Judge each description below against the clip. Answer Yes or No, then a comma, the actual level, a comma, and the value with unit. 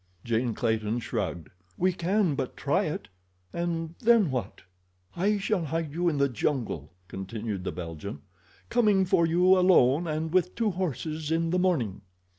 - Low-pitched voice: No, medium, 155 Hz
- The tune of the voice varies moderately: No, wide, 8.2 semitones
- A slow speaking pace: No, average, 150 wpm